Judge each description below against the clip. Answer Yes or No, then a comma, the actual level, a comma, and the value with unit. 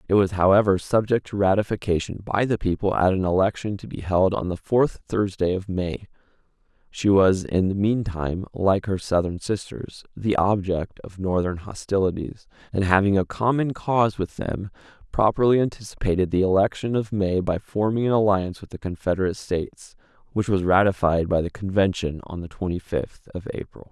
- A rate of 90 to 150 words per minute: No, average, 175 wpm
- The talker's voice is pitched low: Yes, very low, 95 Hz